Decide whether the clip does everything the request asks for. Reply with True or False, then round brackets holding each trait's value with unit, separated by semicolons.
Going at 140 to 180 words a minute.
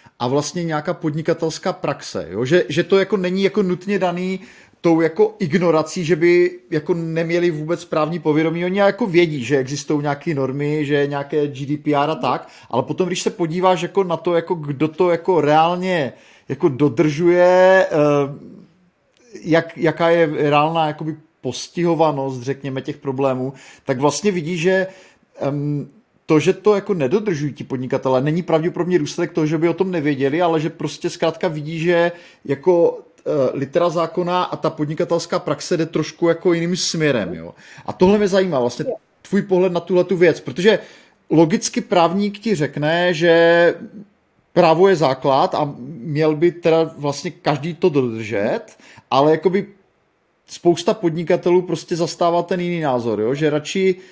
True (155 wpm)